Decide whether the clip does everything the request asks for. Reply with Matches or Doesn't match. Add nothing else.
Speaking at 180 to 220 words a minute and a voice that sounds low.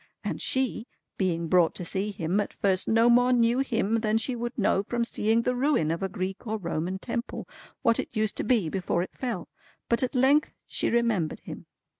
Doesn't match